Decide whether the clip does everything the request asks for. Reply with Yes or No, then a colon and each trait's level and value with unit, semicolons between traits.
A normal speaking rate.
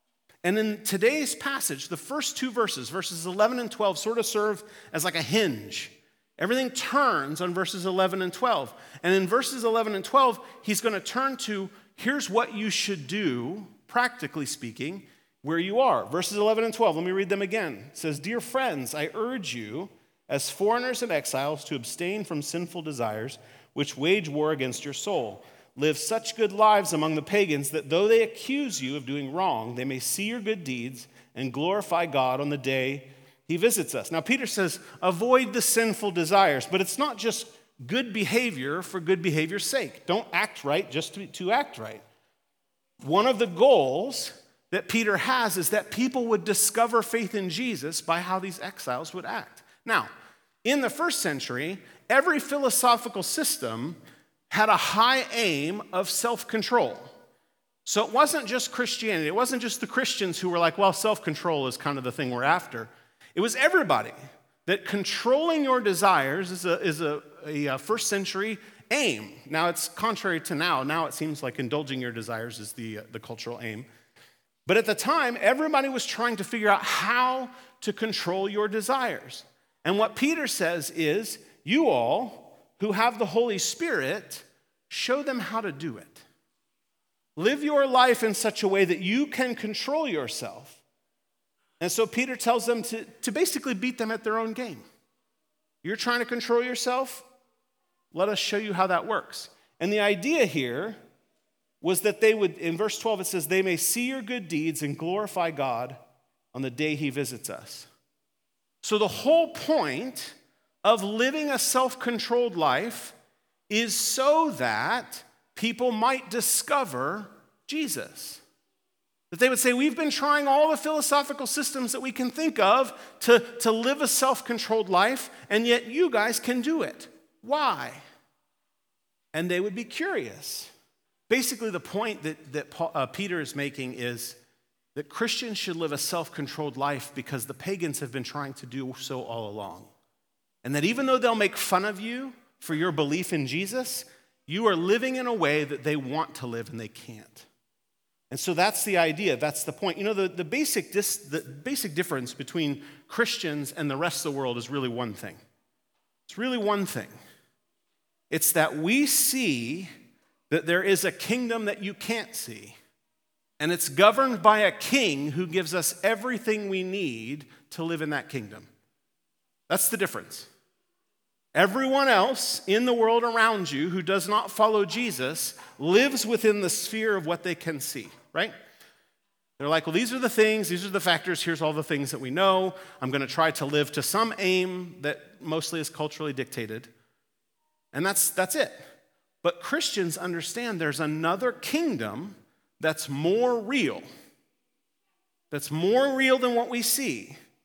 Yes: average, 175 wpm